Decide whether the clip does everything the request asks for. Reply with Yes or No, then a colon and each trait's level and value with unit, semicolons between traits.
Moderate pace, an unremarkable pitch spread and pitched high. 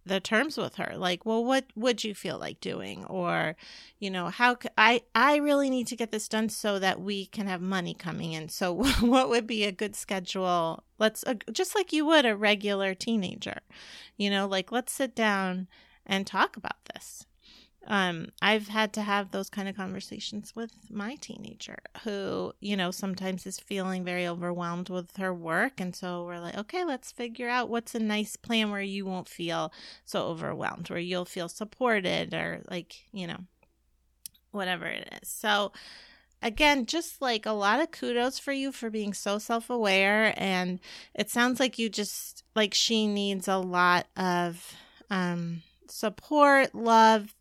Yes: average, 175 wpm; average, 3.8 semitones; high, 205 Hz